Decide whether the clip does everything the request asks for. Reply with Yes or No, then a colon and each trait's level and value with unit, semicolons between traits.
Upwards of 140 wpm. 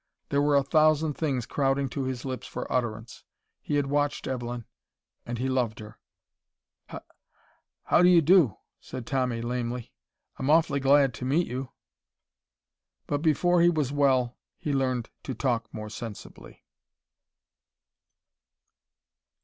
No: slow, 135 wpm